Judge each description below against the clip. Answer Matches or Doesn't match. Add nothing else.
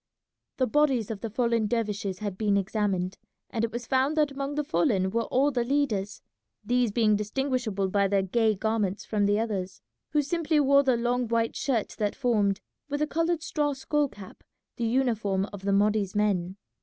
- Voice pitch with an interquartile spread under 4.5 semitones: Doesn't match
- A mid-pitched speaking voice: Doesn't match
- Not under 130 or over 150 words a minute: Doesn't match